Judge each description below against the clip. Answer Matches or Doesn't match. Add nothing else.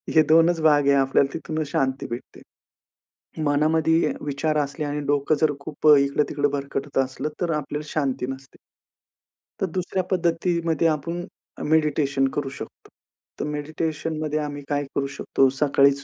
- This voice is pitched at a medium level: Matches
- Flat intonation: Matches